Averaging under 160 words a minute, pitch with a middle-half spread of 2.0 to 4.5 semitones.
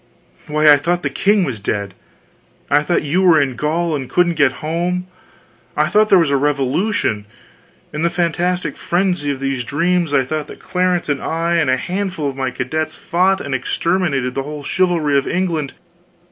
No: average, 185 wpm; average, 4.2 semitones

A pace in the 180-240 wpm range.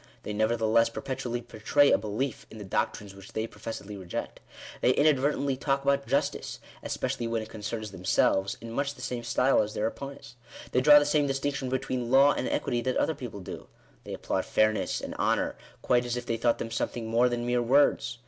Yes: average, 195 wpm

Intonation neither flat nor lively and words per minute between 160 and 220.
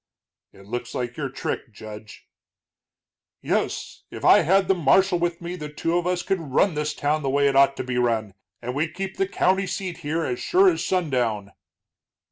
No: wide, 6.3 semitones; average, 195 wpm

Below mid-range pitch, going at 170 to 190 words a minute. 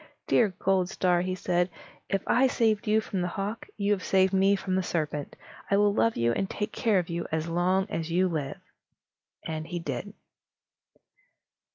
No: medium, 185 Hz; average, 185 wpm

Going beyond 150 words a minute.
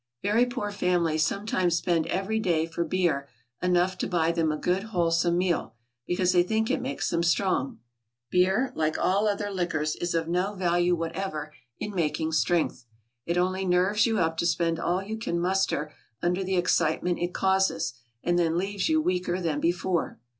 Yes: average, 180 wpm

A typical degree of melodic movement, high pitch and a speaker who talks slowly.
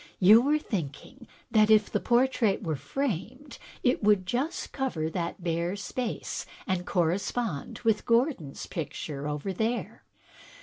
No: wide, 6.4 semitones; high, 205 Hz; slow, 130 wpm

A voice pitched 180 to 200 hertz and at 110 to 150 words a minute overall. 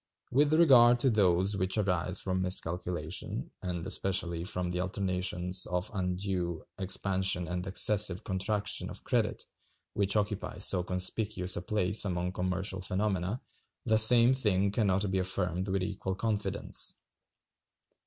No: very low, 95 Hz; slow, 135 wpm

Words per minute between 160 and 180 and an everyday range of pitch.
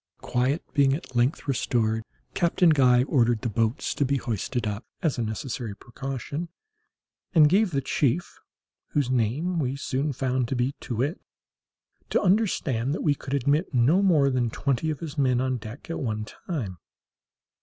Yes: average, 165 wpm; average, 3.7 semitones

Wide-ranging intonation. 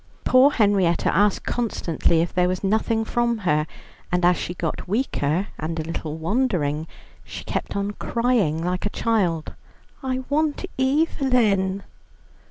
Yes: wide, 6.1 semitones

